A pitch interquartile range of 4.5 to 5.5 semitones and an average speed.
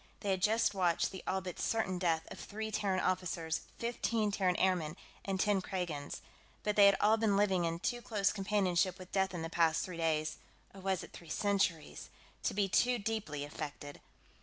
No: average, 3.4 semitones; average, 190 wpm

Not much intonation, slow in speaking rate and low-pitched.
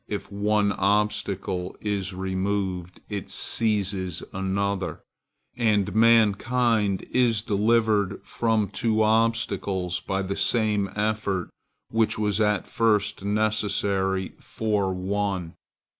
Yes: narrow, 2.1 semitones; slow, 100 wpm; low, 100 Hz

